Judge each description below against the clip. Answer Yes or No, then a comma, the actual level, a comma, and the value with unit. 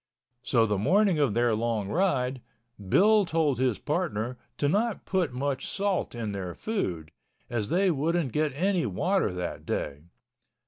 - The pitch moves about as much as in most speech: No, wide, 8.6 semitones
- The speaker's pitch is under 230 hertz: Yes, medium, 140 Hz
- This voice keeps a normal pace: Yes, average, 150 wpm